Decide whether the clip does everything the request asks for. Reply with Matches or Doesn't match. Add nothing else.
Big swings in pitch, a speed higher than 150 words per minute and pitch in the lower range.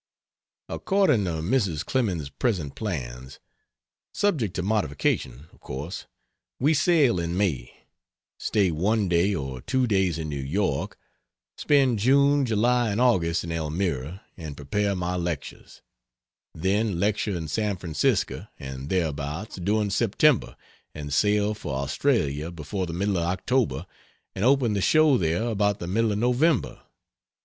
Doesn't match